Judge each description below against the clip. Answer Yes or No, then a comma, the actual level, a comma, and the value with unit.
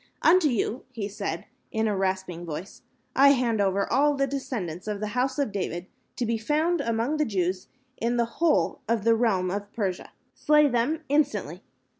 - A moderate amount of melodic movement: No, wide, 5.7 semitones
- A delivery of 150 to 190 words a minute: Yes, average, 180 wpm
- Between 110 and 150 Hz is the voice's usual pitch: No, high, 230 Hz